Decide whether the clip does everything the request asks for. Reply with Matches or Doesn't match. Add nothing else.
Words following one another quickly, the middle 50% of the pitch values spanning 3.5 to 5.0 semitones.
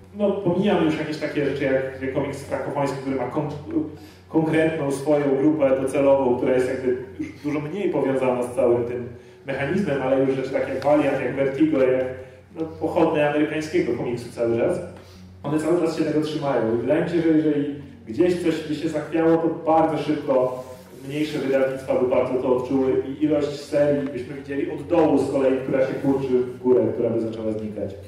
Doesn't match